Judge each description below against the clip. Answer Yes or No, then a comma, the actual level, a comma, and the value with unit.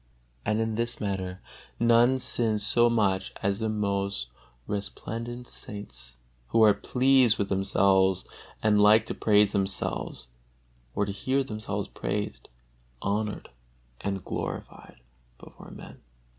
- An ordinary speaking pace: No, slow, 120 wpm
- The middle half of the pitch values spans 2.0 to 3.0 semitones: Yes, average, 2.7 semitones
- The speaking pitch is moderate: No, low, 105 Hz